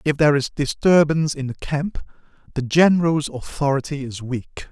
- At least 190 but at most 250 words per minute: No, average, 155 wpm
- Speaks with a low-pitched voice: No, medium, 145 Hz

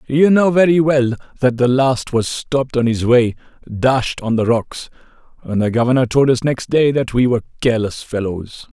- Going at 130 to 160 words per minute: No, average, 190 wpm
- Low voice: Yes, low, 125 Hz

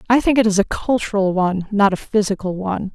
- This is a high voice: Yes, high, 205 Hz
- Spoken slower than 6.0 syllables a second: No, 6.2 syllables/s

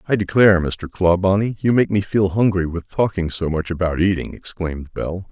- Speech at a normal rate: Yes, average, 190 wpm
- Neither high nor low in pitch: No, very low, 90 Hz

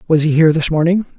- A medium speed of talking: No, fast, 255 wpm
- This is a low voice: No, medium, 160 Hz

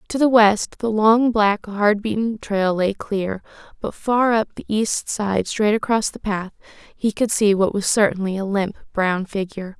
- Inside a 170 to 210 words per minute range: Yes, average, 190 wpm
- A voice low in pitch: No, high, 210 Hz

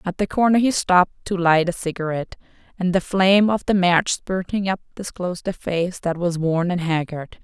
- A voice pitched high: No, medium, 180 Hz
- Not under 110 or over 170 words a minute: No, average, 195 wpm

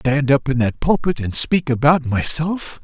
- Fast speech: Yes, fast, 210 wpm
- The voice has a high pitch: No, medium, 140 Hz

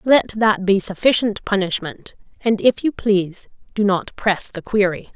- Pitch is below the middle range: No, high, 205 Hz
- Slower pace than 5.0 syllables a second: Yes, 4.5 syllables/s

